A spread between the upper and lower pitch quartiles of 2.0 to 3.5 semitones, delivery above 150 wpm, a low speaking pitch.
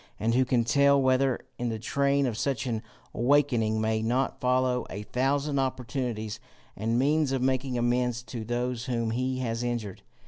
Yes: narrow, 2.5 semitones; average, 170 wpm; low, 125 Hz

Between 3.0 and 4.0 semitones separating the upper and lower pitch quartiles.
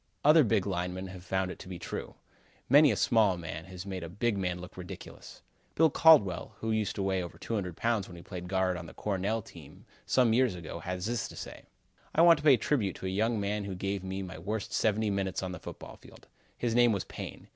Yes: average, 3.5 semitones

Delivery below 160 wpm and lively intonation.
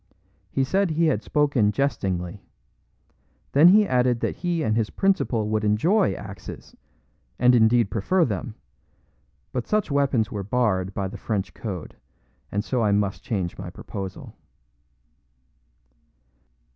Yes: slow, 135 wpm; wide, 5.9 semitones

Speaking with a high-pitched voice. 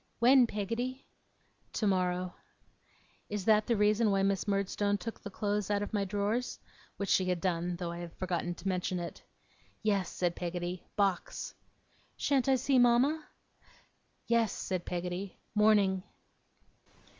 Yes: high, 200 Hz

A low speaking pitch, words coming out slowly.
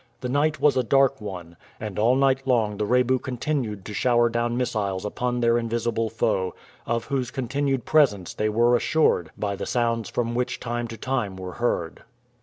No: low, 120 Hz; average, 185 wpm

